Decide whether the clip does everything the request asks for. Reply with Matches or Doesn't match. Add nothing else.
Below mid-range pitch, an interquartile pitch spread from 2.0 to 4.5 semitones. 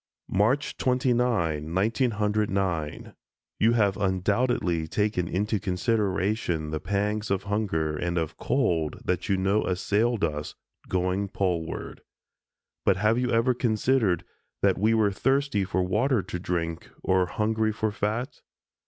Matches